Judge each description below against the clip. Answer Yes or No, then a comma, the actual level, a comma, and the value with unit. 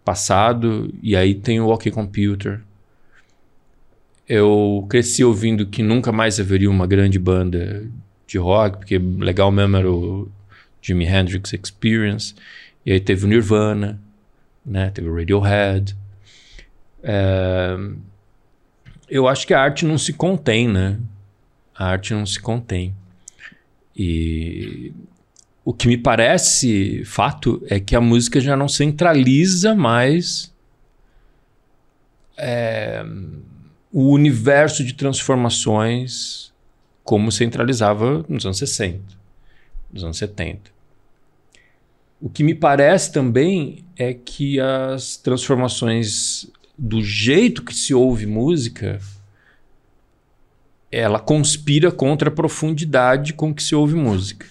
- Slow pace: Yes, slow, 115 wpm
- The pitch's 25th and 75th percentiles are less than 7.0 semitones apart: Yes, wide, 5.4 semitones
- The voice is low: Yes, low, 115 Hz